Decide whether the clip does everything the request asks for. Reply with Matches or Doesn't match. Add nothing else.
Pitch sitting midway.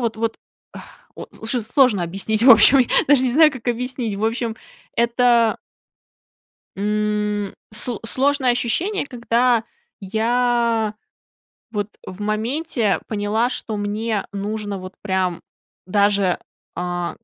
Doesn't match